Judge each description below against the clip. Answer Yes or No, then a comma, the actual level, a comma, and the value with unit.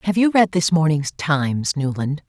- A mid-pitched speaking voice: Yes, medium, 160 Hz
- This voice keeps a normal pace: Yes, average, 185 wpm